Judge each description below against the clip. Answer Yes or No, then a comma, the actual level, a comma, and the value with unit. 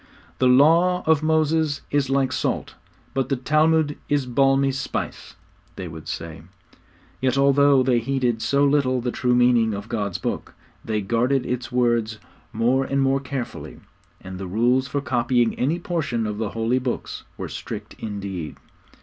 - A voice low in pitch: Yes, low, 130 Hz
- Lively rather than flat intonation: No, average, 3.4 semitones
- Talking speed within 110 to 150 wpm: No, average, 160 wpm